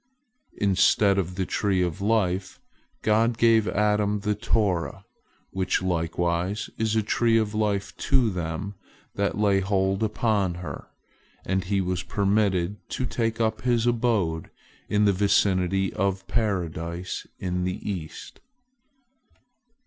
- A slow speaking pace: Yes, slow, 125 wpm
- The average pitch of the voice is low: Yes, low, 100 Hz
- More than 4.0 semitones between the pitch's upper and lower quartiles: No, average, 2.7 semitones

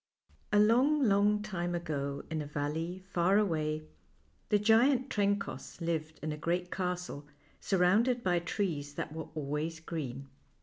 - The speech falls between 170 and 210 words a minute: No, slow, 135 wpm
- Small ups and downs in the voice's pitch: No, average, 4.9 semitones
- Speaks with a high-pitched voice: No, medium, 175 Hz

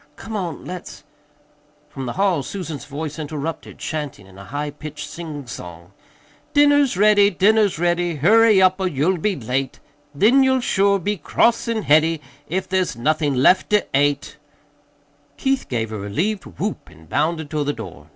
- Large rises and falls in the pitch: Yes, wide, 5.7 semitones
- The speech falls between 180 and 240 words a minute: No, average, 160 wpm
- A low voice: No, medium, 160 Hz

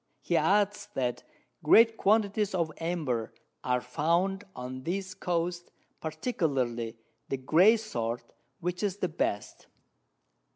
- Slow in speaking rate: Yes, slow, 115 wpm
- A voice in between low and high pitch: Yes, medium, 170 Hz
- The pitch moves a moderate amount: No, wide, 7.1 semitones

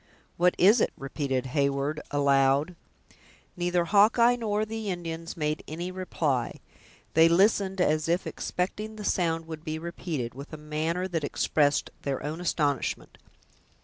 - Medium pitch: Yes, medium, 165 Hz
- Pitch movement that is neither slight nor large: Yes, average, 3.8 semitones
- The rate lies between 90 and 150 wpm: Yes, average, 140 wpm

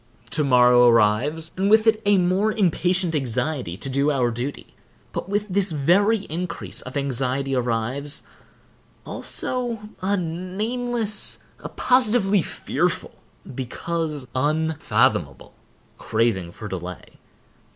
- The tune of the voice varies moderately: No, wide, 7.8 semitones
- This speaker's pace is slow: Yes, slow, 110 wpm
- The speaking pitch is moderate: Yes, medium, 160 Hz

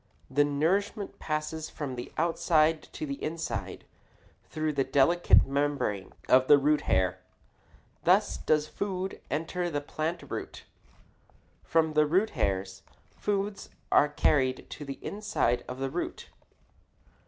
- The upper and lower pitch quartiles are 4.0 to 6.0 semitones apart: No, average, 3.5 semitones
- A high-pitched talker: No, medium, 150 Hz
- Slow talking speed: Yes, slow, 130 wpm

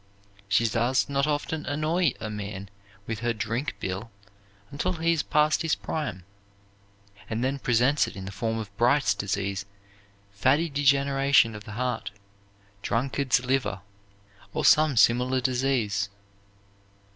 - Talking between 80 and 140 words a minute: Yes, slow, 135 wpm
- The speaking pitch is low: Yes, low, 125 Hz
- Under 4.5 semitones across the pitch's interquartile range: No, average, 4.8 semitones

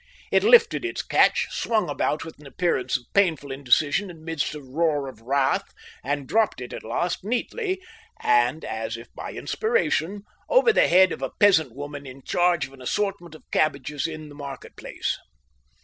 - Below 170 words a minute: No, average, 175 wpm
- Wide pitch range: Yes, wide, 6.4 semitones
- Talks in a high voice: No, medium, 155 Hz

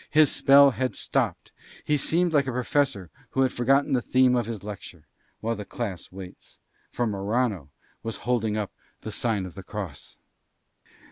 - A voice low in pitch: Yes, low, 115 Hz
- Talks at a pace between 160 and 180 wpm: Yes, average, 165 wpm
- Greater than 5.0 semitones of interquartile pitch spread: No, average, 4.6 semitones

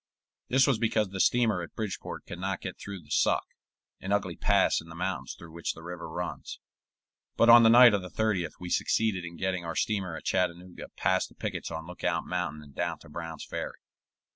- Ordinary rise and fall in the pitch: Yes, average, 4.0 semitones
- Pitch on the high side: No, very low, 90 Hz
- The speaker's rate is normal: No, fast, 210 wpm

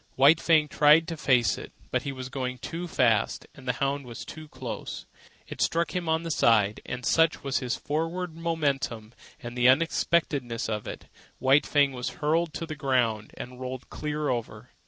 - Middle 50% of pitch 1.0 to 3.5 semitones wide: No, average, 4.4 semitones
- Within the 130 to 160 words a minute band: No, average, 185 wpm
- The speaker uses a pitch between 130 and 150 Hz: Yes, medium, 140 Hz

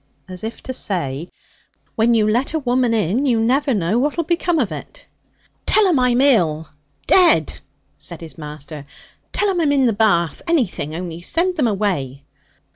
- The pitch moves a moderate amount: No, wide, 8.6 semitones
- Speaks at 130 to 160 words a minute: No, average, 170 wpm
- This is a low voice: No, high, 225 Hz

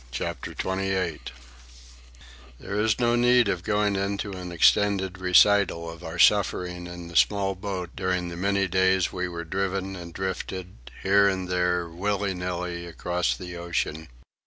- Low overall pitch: Yes, very low, 95 Hz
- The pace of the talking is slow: No, average, 150 wpm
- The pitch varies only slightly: Yes, narrow, 2.0 semitones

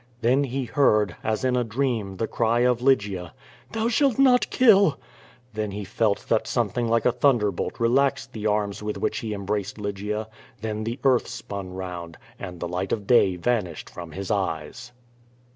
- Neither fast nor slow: Yes, average, 175 wpm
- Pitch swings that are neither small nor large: Yes, average, 4.0 semitones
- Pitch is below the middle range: Yes, low, 110 Hz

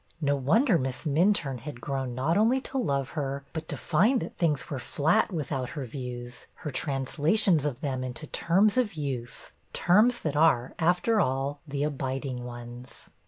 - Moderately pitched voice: Yes, medium, 145 Hz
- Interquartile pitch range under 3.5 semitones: No, average, 4.7 semitones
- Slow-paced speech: No, average, 165 wpm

